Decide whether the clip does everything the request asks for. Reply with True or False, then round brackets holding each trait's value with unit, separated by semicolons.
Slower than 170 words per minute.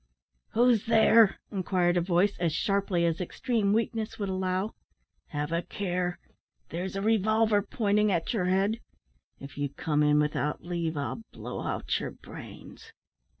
True (150 wpm)